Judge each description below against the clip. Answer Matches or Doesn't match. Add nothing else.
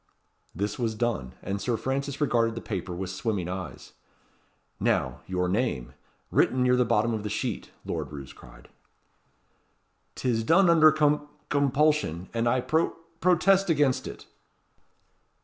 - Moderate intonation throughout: Doesn't match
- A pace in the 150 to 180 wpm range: Doesn't match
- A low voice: Matches